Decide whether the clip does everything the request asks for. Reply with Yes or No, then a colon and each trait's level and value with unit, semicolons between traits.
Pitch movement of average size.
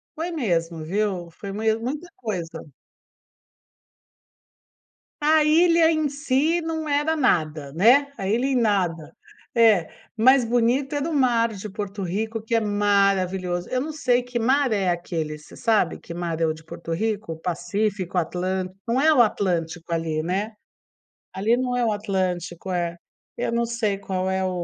No: wide, 6.1 semitones